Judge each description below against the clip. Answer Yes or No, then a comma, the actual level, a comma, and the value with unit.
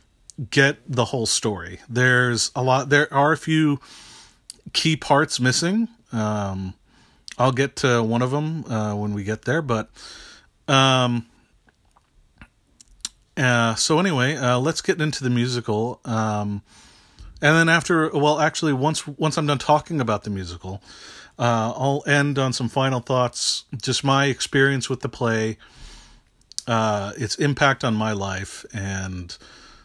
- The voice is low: Yes, low, 125 Hz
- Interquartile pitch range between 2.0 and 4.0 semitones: No, average, 4.8 semitones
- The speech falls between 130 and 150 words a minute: Yes, average, 145 wpm